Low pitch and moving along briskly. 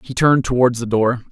Yes: low, 120 Hz; fast, 230 wpm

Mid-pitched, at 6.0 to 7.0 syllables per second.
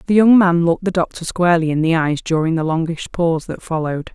Yes: medium, 170 Hz; 6.3 syllables/s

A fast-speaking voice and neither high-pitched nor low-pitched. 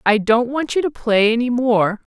No: fast, 225 wpm; high, 235 Hz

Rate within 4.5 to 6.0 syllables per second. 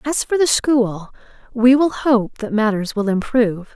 No: 4.3 syllables/s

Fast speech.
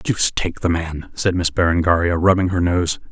No: average, 190 wpm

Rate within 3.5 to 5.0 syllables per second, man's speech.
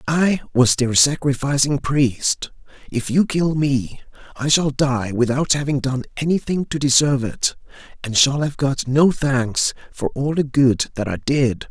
Yes: 4.2 syllables/s; male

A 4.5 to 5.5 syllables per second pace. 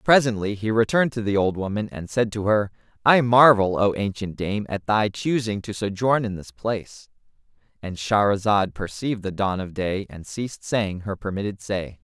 Yes: 5.0 syllables/s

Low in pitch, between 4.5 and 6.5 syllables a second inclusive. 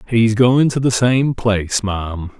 No: low, 110 Hz; 4.1 syllables/s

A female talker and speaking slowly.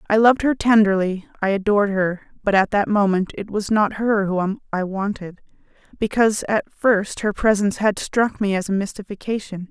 No: female; average, 180 wpm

